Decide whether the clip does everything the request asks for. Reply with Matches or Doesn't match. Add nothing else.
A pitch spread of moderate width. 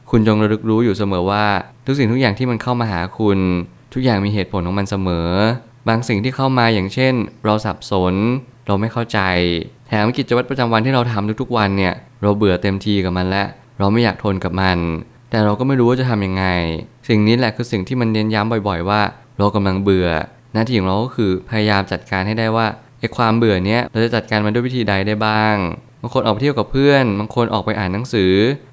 Matches